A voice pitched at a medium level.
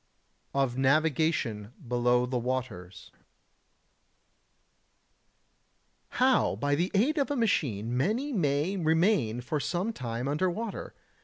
Yes: medium, 145 Hz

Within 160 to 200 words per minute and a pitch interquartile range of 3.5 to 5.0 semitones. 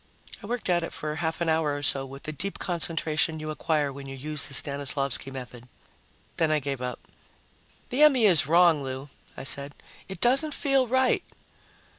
Yes: average, 185 wpm; average, 4.1 semitones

